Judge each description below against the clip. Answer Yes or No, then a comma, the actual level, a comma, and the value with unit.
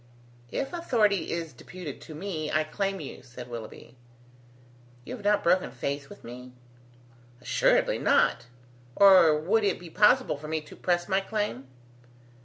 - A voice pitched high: No, medium, 170 Hz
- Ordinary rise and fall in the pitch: No, wide, 6.1 semitones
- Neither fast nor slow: Yes, average, 150 wpm